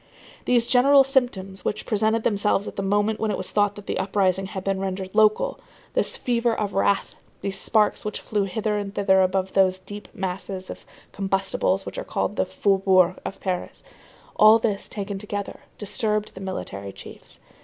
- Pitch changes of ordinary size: No, narrow, 2.0 semitones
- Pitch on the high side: Yes, high, 200 Hz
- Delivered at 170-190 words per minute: Yes, average, 175 wpm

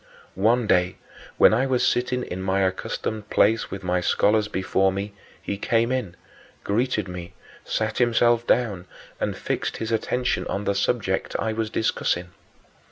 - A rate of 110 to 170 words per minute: Yes, average, 160 wpm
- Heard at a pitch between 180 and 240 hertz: No, low, 105 Hz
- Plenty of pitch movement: No, average, 3.7 semitones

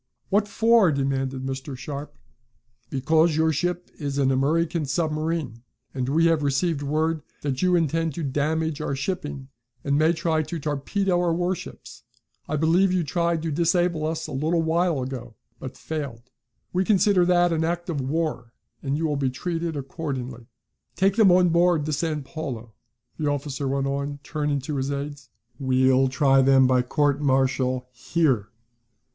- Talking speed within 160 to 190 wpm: Yes, average, 165 wpm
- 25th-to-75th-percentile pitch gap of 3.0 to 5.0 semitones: Yes, average, 3.7 semitones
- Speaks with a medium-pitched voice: Yes, medium, 150 Hz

